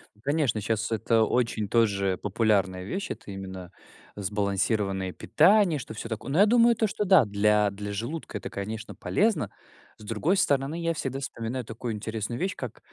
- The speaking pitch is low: Yes, low, 115 Hz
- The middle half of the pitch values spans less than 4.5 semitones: No, wide, 6.2 semitones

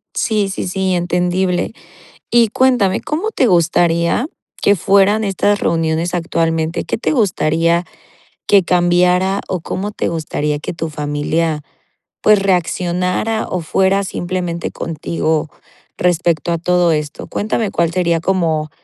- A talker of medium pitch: Yes, medium, 175 Hz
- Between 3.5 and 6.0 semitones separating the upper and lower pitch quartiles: No, average, 2.8 semitones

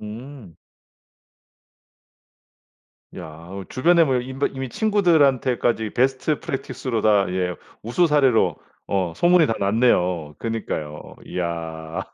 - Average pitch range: No, wide, 6.5 semitones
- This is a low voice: Yes, low, 115 Hz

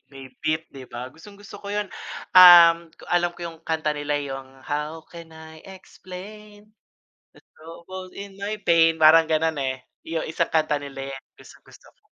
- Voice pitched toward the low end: No, medium, 165 Hz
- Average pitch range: Yes, average, 3.5 semitones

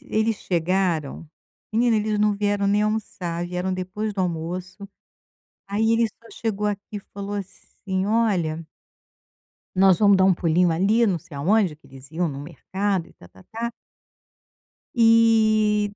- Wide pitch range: No, average, 3.5 semitones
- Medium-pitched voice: No, high, 195 Hz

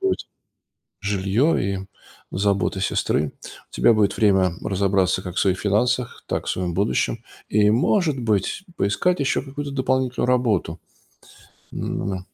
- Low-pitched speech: Yes, low, 105 Hz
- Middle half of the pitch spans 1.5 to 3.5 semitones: No, average, 4.9 semitones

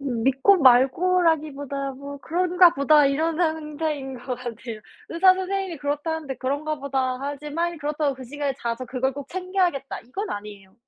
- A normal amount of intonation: Yes, average, 3.7 semitones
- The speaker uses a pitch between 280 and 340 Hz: Yes, very high, 285 Hz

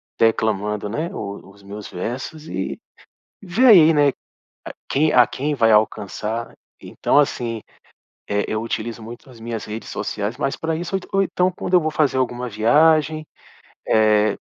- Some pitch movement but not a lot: No, wide, 6.4 semitones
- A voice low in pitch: Yes, low, 120 Hz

